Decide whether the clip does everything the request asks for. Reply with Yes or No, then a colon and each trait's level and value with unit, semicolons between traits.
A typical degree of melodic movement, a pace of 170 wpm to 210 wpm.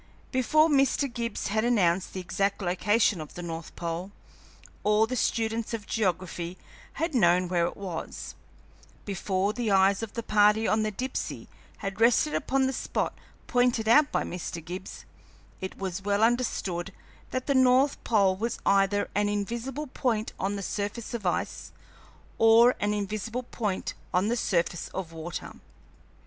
No: average, 4.0 semitones; average, 155 wpm